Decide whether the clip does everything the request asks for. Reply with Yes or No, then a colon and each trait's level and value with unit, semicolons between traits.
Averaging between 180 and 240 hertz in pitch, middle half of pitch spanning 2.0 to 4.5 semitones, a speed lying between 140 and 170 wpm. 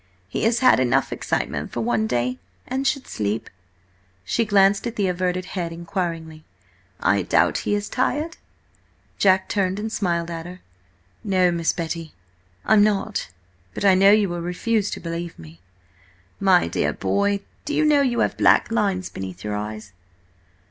Yes: medium, 185 Hz; average, 4.1 semitones; average, 160 wpm